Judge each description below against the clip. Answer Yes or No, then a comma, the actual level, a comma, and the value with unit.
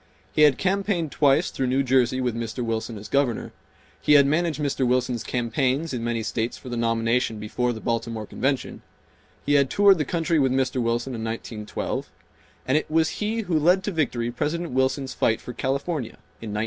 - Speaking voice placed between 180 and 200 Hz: No, low, 130 Hz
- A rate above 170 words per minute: Yes, average, 190 wpm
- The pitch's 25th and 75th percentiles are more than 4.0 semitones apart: Yes, average, 4.5 semitones